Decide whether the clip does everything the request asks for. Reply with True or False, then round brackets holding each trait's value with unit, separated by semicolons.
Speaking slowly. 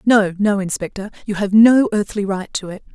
False (205 wpm)